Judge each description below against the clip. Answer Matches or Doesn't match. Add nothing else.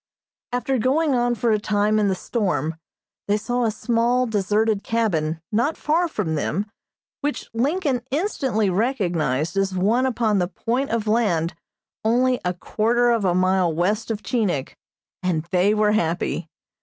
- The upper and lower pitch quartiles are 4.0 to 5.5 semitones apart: Matches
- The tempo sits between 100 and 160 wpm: Matches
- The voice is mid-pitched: Doesn't match